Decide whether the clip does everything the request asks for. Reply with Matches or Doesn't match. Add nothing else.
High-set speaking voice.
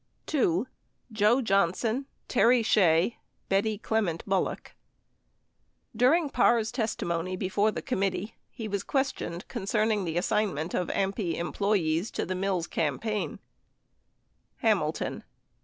Matches